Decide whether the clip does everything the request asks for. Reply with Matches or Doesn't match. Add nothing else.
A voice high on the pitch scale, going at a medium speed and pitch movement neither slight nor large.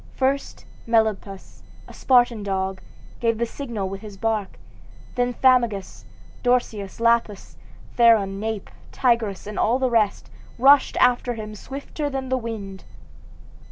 Doesn't match